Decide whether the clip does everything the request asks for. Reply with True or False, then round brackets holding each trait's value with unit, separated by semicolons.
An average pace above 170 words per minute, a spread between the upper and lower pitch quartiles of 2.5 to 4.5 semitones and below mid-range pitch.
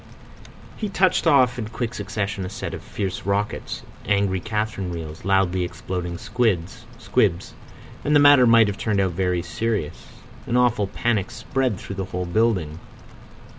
False (145 wpm; 4.2 semitones; 105 Hz)